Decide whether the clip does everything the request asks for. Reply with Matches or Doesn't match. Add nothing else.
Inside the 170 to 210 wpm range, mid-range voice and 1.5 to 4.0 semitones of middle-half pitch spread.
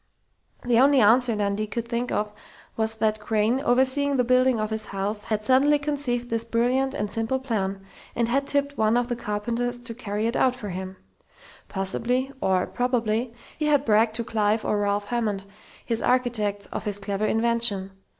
Doesn't match